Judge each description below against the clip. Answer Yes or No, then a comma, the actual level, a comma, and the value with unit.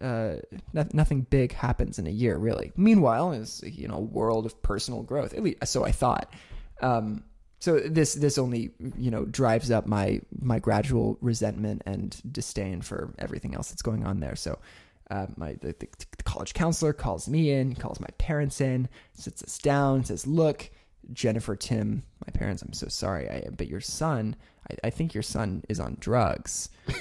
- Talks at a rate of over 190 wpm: No, average, 185 wpm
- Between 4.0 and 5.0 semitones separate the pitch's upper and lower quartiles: Yes, average, 4.5 semitones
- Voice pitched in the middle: No, low, 120 Hz